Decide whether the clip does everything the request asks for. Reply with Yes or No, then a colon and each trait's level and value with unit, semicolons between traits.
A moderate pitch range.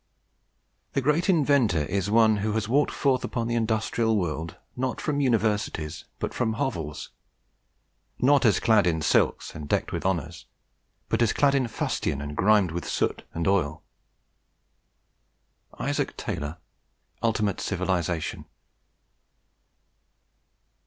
No: wide, 6.1 semitones